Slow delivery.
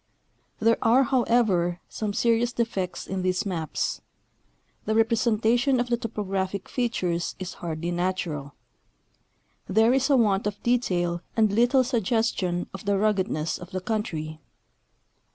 Yes: slow, 130 wpm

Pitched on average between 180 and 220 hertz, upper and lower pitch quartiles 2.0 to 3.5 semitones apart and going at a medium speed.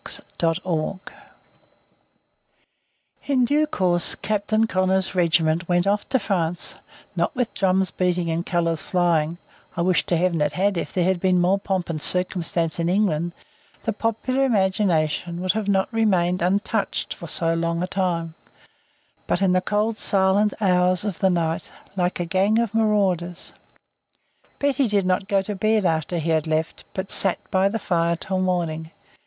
Yes: medium, 185 Hz; average, 2.9 semitones; average, 160 wpm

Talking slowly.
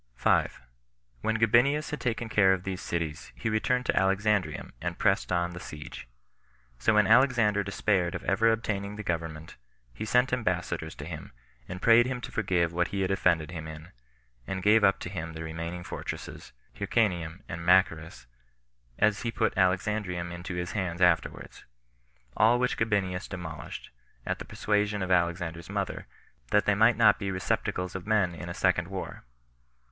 No: average, 170 wpm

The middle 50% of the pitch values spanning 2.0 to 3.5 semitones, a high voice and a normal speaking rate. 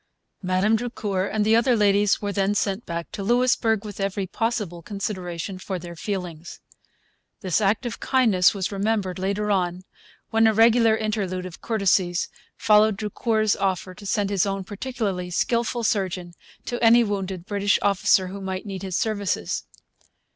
Yes: average, 2.8 semitones; high, 200 Hz; average, 155 wpm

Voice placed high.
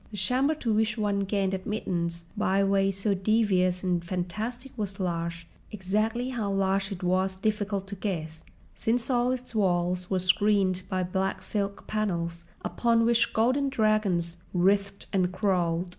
Yes: high, 195 Hz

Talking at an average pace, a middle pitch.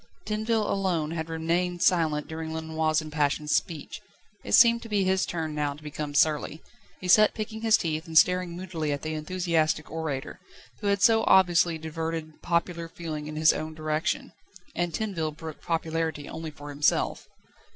Yes: average, 165 wpm; medium, 160 Hz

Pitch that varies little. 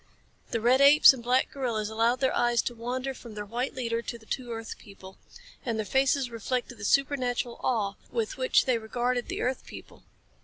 Yes: narrow, 2.2 semitones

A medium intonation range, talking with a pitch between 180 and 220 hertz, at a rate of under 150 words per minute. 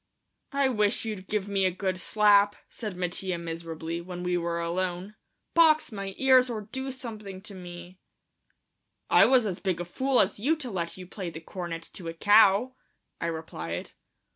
No: average, 3.8 semitones; high, 190 Hz; average, 175 wpm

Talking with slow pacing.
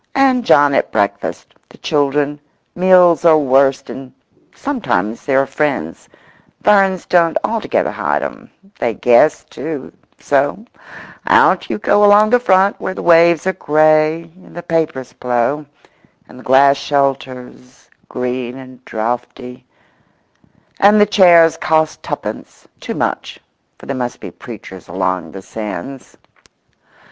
Yes: slow, 120 wpm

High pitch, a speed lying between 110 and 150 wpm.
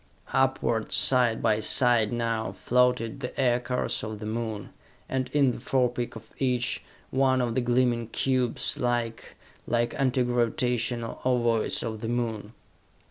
No: low, 120 Hz; slow, 135 wpm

